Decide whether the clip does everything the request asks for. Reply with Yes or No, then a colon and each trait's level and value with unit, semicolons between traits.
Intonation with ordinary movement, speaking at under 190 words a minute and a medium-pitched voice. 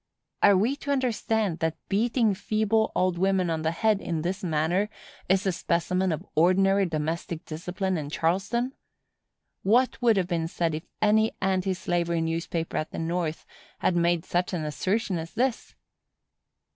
Yes: average, 3.9 semitones; average, 160 wpm; medium, 180 Hz